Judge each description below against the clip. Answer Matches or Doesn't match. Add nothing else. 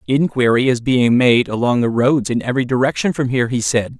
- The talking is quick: Matches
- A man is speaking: Matches